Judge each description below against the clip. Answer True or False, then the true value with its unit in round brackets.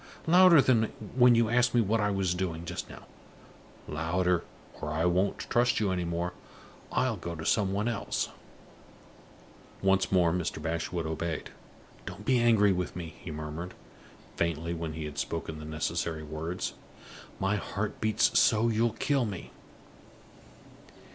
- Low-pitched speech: True (90 Hz)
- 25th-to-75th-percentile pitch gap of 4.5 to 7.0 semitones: True (5.0 semitones)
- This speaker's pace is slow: False (150 wpm)